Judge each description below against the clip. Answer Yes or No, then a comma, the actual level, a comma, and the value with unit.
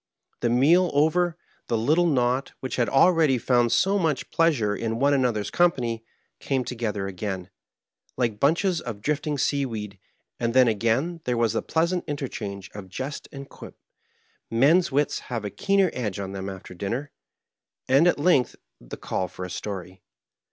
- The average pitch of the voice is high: No, low, 125 Hz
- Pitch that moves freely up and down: Yes, wide, 6.2 semitones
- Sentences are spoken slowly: No, average, 165 wpm